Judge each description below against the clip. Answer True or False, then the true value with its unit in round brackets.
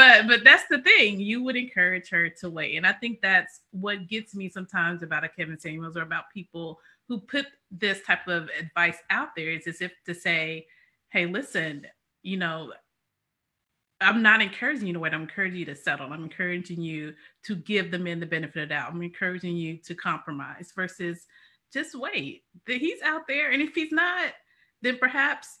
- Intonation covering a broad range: True (6.1 semitones)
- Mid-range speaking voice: True (180 Hz)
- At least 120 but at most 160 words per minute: False (195 wpm)